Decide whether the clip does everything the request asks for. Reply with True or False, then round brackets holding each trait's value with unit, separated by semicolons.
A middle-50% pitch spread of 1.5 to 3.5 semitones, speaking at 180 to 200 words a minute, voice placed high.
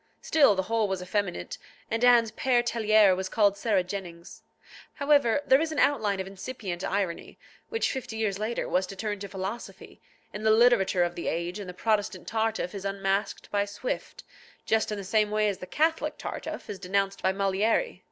True (3.0 semitones; 190 wpm; 205 Hz)